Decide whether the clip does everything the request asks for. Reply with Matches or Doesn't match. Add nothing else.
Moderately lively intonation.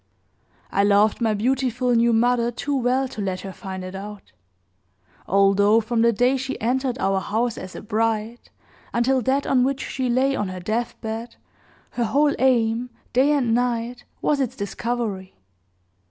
Matches